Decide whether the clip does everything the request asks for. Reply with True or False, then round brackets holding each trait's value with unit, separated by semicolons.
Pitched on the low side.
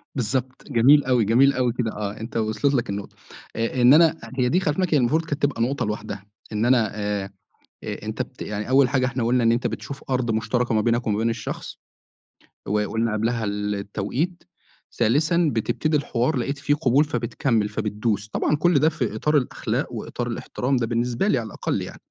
True (120 Hz)